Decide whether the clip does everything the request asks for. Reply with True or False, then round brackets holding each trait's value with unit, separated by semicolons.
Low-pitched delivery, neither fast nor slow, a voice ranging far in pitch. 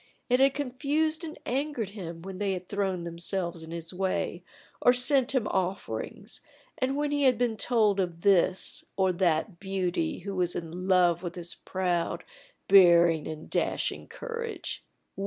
False (190 Hz; 155 wpm; 6.3 semitones)